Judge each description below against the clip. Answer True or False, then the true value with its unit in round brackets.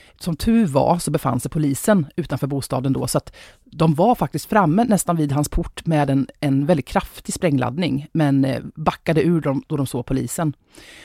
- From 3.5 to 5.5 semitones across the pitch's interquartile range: True (4.2 semitones)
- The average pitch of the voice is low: False (155 Hz)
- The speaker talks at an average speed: True (185 wpm)